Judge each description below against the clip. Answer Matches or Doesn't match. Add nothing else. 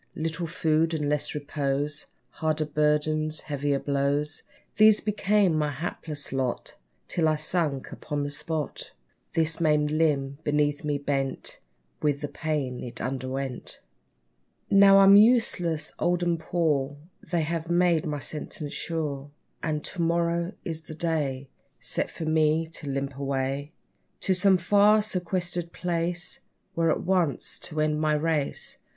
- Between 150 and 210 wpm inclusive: Doesn't match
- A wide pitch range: Doesn't match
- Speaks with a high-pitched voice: Doesn't match